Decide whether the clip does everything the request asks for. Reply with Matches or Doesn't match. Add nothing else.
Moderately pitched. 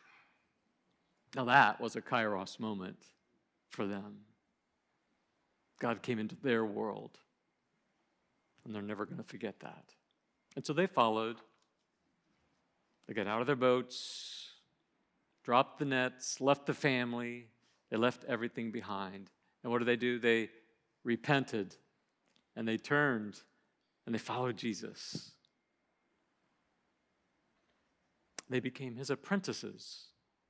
Doesn't match